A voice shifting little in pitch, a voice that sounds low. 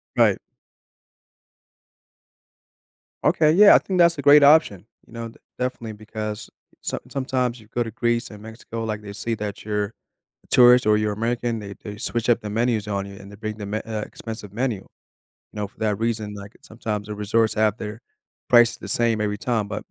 Yes: narrow, 2.2 semitones; low, 110 Hz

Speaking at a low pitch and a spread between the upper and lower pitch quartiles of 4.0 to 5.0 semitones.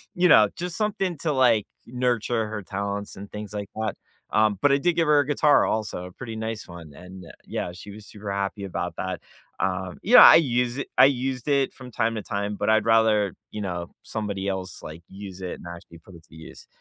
Yes: low, 105 Hz; average, 4.6 semitones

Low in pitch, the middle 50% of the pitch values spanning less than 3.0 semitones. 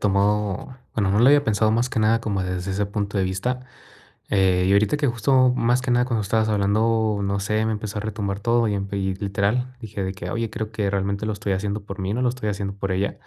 Yes: low, 105 Hz; narrow, 2.5 semitones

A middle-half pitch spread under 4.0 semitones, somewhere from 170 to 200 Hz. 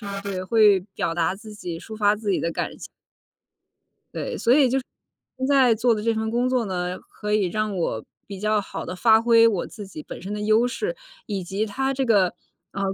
No: average, 3.2 semitones; high, 215 Hz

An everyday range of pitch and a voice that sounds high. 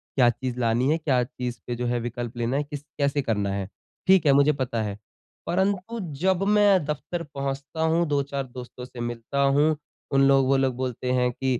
No: average, 3.3 semitones; low, 135 Hz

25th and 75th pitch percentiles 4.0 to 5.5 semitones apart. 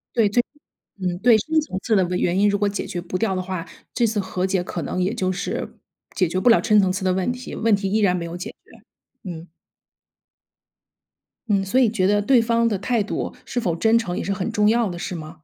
No: average, 3.6 semitones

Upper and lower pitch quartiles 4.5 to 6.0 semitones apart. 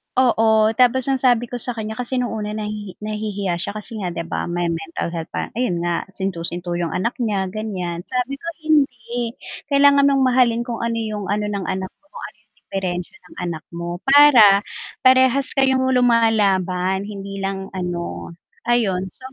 Yes: average, 4.9 semitones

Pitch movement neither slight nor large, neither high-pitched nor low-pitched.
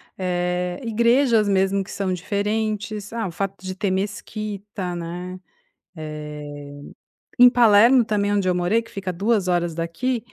No: average, 3.0 semitones; high, 200 Hz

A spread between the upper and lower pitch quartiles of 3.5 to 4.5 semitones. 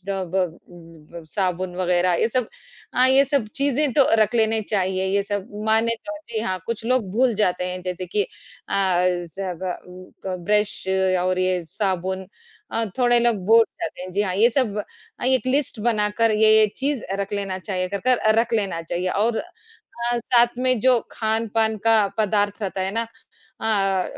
Yes: average, 3.8 semitones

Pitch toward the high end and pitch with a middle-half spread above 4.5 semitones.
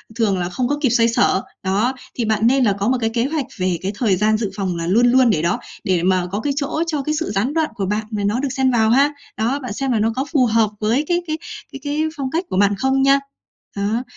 Yes: high, 230 Hz; average, 5.0 semitones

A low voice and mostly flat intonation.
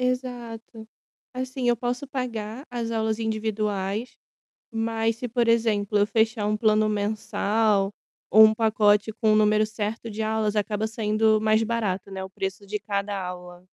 No: high, 220 Hz; narrow, 1.6 semitones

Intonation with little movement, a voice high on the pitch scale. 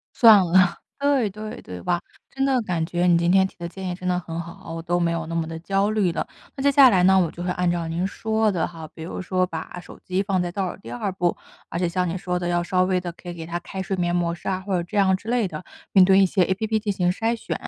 No: narrow, 2.2 semitones; medium, 180 Hz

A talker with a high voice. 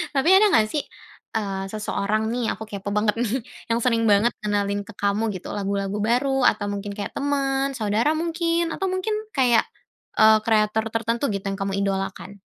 Yes: high, 220 Hz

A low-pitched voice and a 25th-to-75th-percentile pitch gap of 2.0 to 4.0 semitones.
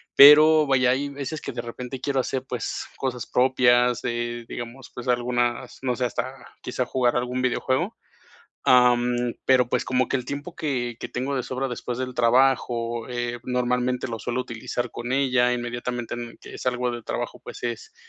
No: low, 125 Hz; narrow, 1.3 semitones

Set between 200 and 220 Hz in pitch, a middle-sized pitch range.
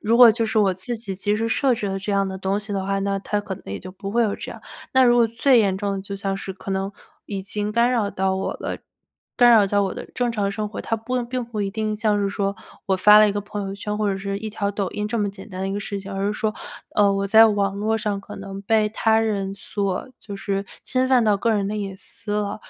No: high, 205 Hz; narrow, 2.0 semitones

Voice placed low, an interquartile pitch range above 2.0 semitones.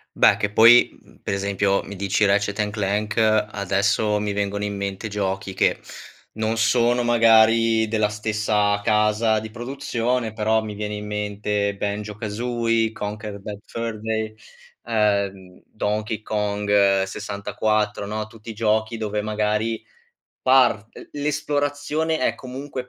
No: low, 105 Hz; narrow, 1.7 semitones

